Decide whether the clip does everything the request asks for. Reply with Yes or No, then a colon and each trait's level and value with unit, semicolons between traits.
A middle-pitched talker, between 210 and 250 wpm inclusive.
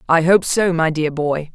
Yes: medium, 165 Hz; fast, 235 wpm